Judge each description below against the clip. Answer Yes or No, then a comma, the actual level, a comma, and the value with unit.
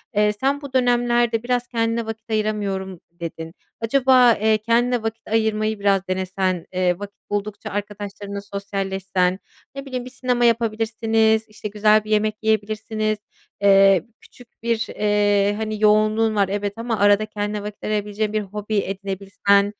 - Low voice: No, high, 215 Hz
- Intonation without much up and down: Yes, narrow, 1.9 semitones